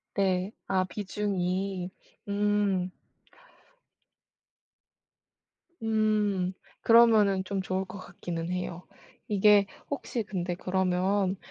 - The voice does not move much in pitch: Yes, narrow, 2.1 semitones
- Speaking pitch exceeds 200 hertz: No, high, 195 Hz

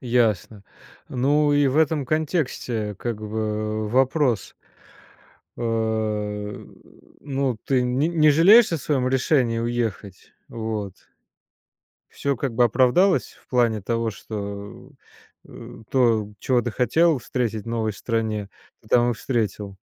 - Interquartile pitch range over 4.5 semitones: No, average, 3.7 semitones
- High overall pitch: No, low, 120 Hz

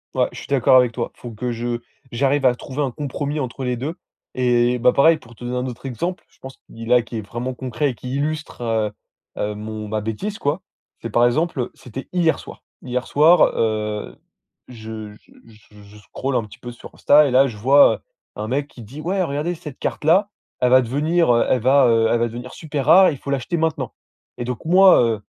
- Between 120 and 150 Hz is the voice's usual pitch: Yes, low, 125 Hz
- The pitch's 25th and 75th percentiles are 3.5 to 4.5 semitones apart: Yes, average, 3.8 semitones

